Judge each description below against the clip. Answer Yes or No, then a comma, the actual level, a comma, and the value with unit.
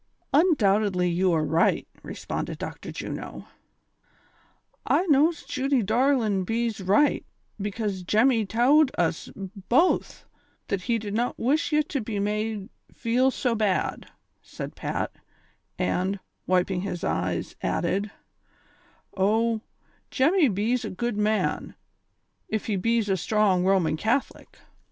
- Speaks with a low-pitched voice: No, high, 215 Hz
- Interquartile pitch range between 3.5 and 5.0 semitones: Yes, average, 4.5 semitones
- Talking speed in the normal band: No, slow, 125 wpm